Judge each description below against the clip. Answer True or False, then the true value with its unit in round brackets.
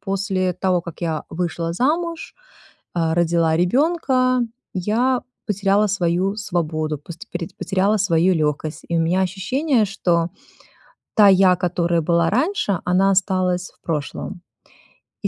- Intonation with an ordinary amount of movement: True (3.2 semitones)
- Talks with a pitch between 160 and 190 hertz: True (185 Hz)